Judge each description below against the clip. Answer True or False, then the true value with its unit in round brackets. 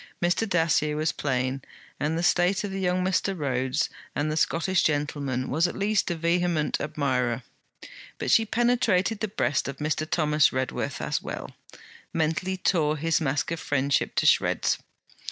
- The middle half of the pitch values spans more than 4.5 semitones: False (4.0 semitones)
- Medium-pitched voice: True (160 Hz)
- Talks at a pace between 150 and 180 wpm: True (155 wpm)